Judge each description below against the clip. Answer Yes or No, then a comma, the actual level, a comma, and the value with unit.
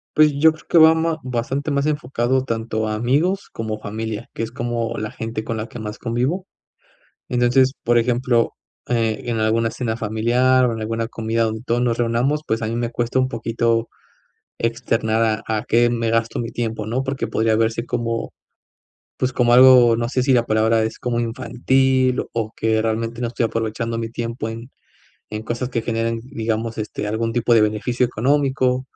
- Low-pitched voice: Yes, low, 115 Hz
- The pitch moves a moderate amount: No, narrow, 1.9 semitones